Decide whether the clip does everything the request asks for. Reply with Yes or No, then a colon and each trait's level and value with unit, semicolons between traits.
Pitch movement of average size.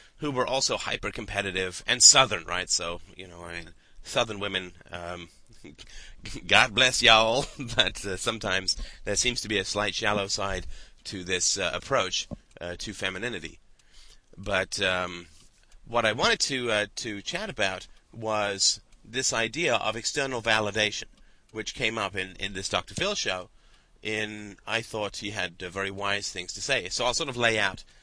Yes: average, 3.5 semitones